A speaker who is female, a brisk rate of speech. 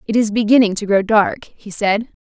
Yes: female; fast, 215 wpm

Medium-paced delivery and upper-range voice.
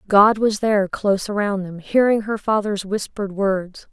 Yes: average, 170 wpm; high, 205 Hz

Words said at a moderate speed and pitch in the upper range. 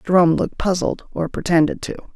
No: average, 165 wpm; medium, 175 Hz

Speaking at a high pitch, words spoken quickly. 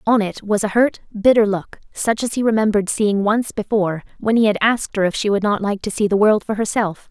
Yes: high, 210 Hz; fast, 255 wpm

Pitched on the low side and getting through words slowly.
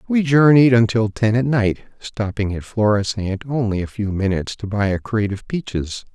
No: low, 110 Hz; average, 185 wpm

